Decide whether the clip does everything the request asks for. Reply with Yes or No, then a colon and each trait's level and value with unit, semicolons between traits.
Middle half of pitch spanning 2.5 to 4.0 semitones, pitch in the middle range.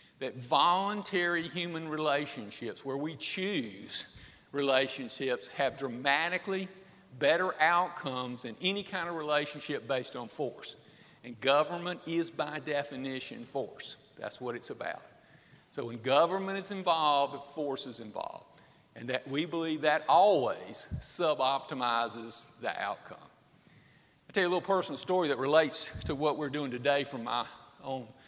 No: average, 4.5 semitones; medium, 150 Hz